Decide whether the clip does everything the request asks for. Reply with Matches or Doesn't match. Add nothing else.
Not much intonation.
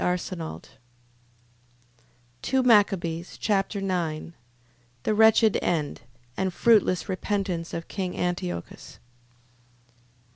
Doesn't match